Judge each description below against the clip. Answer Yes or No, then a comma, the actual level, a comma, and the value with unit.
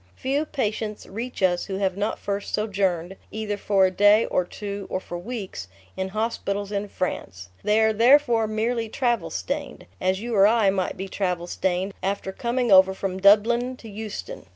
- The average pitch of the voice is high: Yes, high, 205 Hz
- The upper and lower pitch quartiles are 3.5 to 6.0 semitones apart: No, average, 2.8 semitones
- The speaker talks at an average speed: Yes, average, 175 wpm